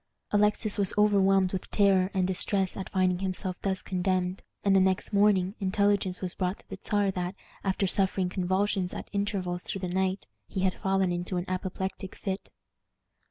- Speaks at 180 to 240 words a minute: No, average, 170 wpm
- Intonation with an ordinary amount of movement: No, narrow, 1.3 semitones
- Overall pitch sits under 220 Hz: Yes, high, 190 Hz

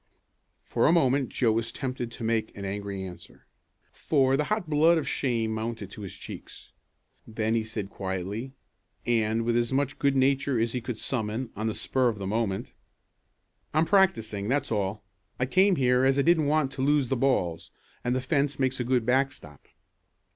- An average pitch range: Yes, average, 3.9 semitones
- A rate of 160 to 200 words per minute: Yes, average, 185 wpm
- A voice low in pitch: Yes, low, 125 Hz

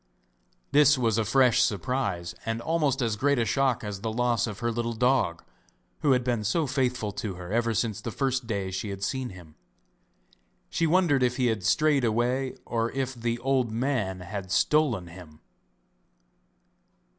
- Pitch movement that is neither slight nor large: Yes, average, 4.1 semitones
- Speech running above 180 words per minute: No, average, 170 wpm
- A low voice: Yes, low, 120 Hz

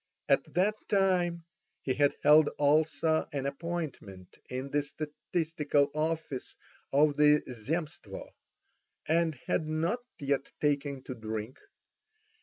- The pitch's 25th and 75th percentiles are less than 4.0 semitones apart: Yes, average, 2.8 semitones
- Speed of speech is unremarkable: No, slow, 110 wpm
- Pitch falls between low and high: Yes, medium, 150 Hz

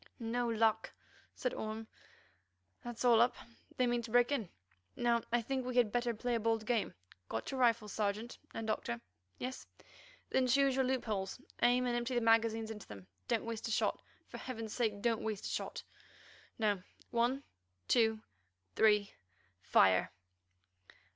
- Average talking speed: Yes, average, 150 wpm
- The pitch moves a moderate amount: No, narrow, 2.3 semitones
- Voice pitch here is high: Yes, high, 230 Hz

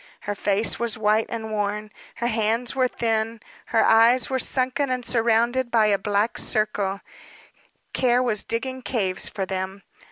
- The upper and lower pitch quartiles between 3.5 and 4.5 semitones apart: No, narrow, 2.6 semitones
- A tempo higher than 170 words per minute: No, average, 155 wpm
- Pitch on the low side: No, high, 225 Hz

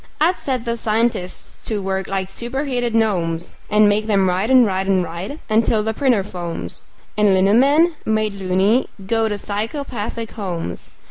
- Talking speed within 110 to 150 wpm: No, average, 160 wpm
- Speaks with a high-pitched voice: Yes, high, 210 Hz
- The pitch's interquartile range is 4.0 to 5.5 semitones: No, average, 3.6 semitones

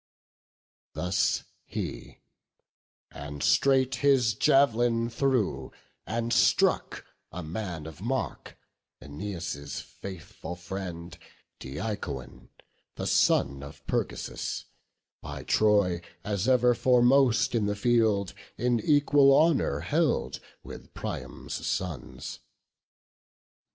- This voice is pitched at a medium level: No, low, 105 Hz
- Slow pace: Yes, slow, 90 wpm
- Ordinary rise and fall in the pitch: No, wide, 6.4 semitones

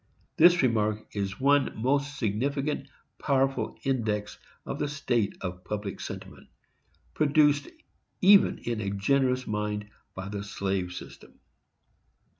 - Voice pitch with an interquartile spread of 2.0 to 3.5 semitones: No, wide, 5.4 semitones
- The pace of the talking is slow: Yes, slow, 115 wpm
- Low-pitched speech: Yes, low, 115 Hz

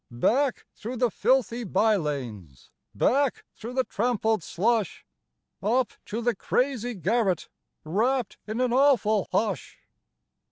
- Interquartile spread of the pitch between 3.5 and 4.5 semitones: Yes, average, 4.2 semitones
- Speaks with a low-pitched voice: No, high, 225 Hz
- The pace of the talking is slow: Yes, slow, 125 wpm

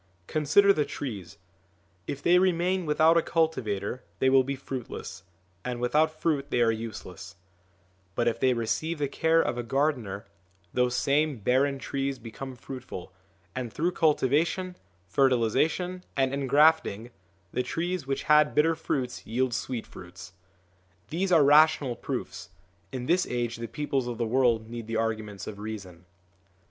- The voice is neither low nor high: No, low, 130 Hz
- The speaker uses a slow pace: No, average, 150 wpm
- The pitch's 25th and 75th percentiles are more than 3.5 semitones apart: Yes, average, 5.1 semitones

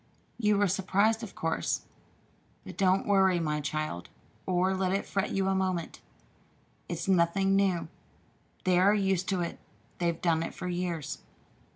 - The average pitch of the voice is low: No, medium, 185 Hz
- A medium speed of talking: Yes, average, 160 wpm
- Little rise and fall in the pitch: Yes, narrow, 2.3 semitones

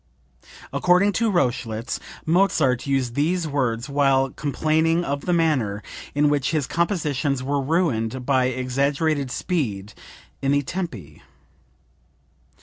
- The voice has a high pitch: No, medium, 140 Hz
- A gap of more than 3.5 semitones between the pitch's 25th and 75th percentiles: Yes, average, 4.2 semitones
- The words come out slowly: Yes, slow, 115 wpm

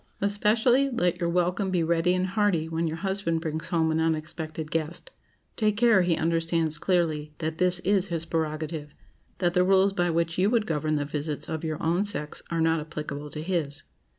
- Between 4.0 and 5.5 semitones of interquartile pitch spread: No, average, 2.8 semitones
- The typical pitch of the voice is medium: Yes, medium, 165 Hz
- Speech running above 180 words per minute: Yes, average, 190 wpm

